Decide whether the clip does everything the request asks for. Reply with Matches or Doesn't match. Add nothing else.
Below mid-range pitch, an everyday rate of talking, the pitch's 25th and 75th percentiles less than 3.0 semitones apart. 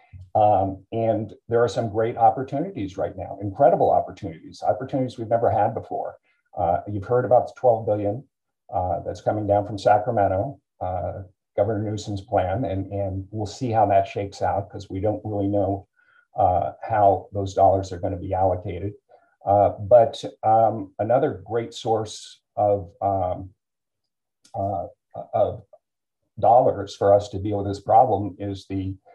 Matches